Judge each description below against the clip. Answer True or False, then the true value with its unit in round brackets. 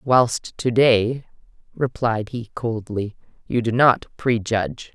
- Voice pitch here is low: True (115 Hz)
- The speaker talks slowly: True (120 wpm)